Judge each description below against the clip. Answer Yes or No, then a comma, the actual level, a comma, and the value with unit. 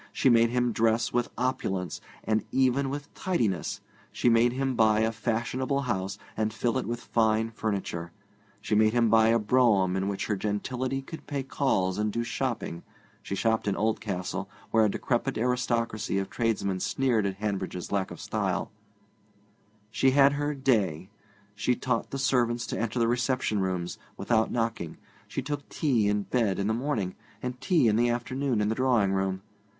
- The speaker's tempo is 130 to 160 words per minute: No, average, 175 wpm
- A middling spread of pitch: Yes, average, 3.6 semitones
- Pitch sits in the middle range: No, low, 115 Hz